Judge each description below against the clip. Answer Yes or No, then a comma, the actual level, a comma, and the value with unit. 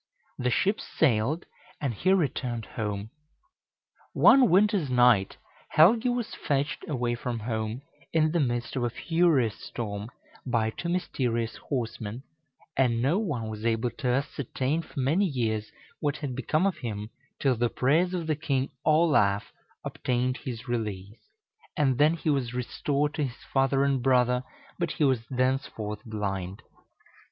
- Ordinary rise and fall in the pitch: Yes, average, 4.8 semitones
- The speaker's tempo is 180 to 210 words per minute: No, average, 145 wpm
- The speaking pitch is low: Yes, low, 130 Hz